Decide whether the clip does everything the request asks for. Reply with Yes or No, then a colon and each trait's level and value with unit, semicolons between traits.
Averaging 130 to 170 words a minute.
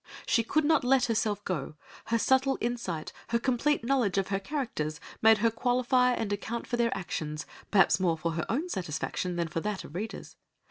No: average, 190 wpm